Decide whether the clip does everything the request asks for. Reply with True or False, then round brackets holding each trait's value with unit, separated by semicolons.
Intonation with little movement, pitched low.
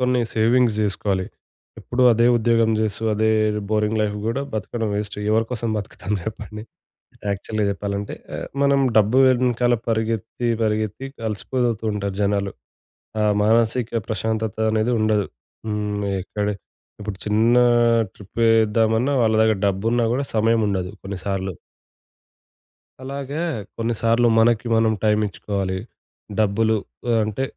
True (1.9 semitones; 110 Hz)